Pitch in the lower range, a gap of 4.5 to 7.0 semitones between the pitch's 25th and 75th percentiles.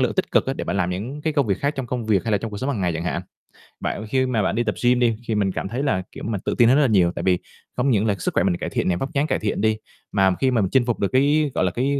Yes: low, 115 Hz; average, 5.3 semitones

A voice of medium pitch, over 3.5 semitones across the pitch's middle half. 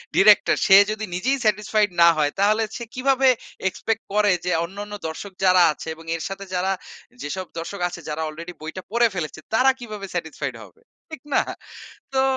No: high, 200 Hz; average, 3.9 semitones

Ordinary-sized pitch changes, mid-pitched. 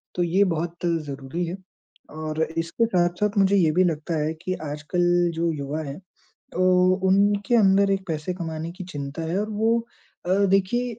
Yes: average, 3.5 semitones; medium, 175 Hz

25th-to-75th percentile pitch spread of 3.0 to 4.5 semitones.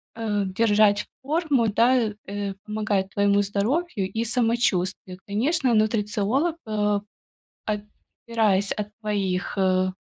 No: narrow, 2.5 semitones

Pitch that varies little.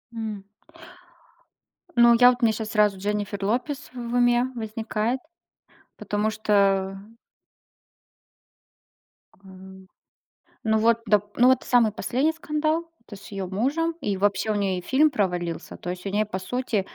No: average, 3.7 semitones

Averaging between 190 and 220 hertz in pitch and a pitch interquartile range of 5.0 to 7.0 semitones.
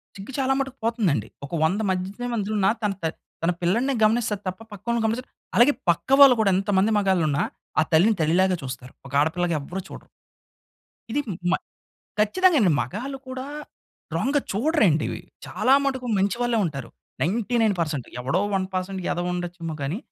Yes: high, 195 Hz; wide, 5.5 semitones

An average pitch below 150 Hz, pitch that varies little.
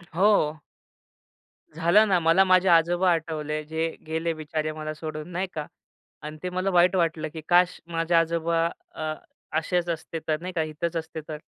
No: medium, 165 Hz; narrow, 2.0 semitones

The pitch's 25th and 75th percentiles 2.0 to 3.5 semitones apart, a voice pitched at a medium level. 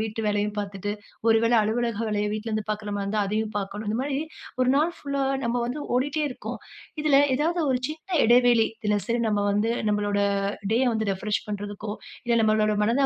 No: average, 2.9 semitones; high, 220 Hz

